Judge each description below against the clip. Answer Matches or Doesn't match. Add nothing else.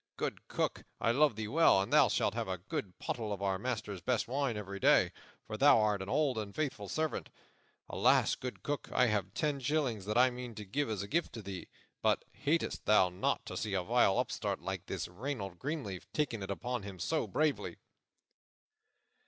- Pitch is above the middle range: Doesn't match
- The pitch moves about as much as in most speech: Doesn't match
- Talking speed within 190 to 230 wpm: Matches